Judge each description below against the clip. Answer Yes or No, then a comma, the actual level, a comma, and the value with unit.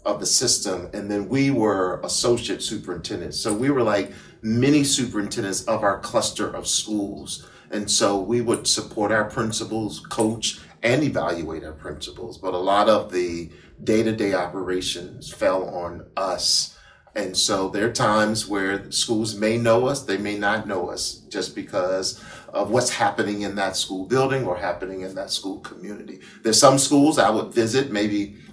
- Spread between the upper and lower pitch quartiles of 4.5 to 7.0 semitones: No, average, 3.1 semitones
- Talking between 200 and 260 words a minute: No, average, 170 wpm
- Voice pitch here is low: Yes, low, 105 Hz